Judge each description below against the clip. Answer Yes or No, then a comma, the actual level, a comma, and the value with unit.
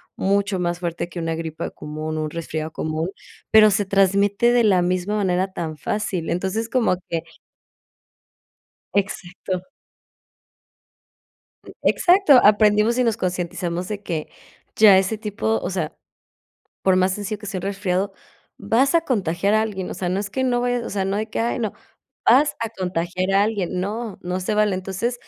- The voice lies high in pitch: Yes, high, 195 Hz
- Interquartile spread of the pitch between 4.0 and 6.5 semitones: No, average, 3.3 semitones